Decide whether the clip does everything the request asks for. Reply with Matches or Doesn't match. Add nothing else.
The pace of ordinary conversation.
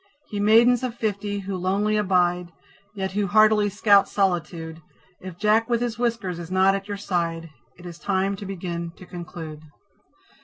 Matches